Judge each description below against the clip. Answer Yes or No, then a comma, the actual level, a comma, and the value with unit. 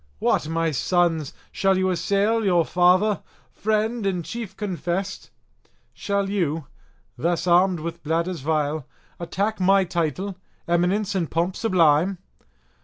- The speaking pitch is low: No, medium, 180 Hz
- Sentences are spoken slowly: Yes, slow, 120 wpm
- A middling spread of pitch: Yes, average, 3.0 semitones